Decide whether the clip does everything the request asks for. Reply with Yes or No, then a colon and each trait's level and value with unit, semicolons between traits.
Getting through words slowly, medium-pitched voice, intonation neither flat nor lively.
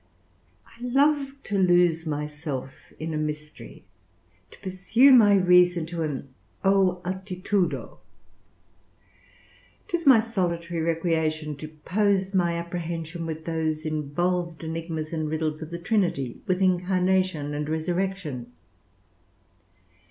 Yes: slow, 110 wpm; medium, 170 Hz; average, 3.2 semitones